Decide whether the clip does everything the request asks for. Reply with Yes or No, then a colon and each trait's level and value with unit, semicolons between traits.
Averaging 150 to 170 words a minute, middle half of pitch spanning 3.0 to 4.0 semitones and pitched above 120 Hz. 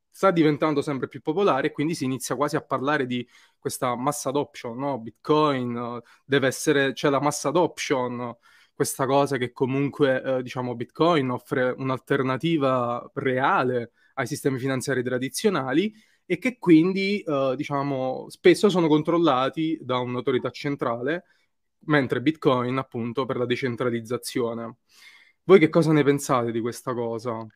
No: average, 140 wpm; average, 3.4 semitones; low, 135 Hz